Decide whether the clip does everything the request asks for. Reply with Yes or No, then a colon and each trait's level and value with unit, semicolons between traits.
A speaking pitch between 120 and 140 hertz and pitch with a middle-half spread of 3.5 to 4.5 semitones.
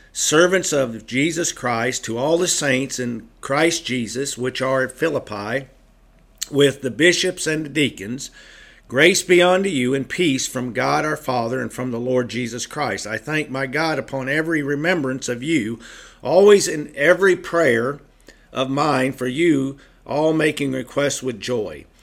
Yes: low, 135 Hz; average, 4.0 semitones